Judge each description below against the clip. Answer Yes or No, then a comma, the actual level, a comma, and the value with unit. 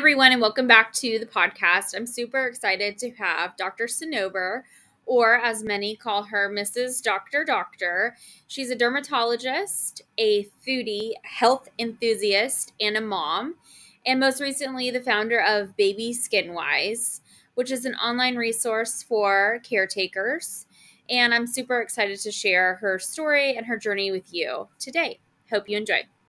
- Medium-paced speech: Yes, average, 150 wpm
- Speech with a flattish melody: No, average, 3.4 semitones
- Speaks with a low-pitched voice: No, high, 230 Hz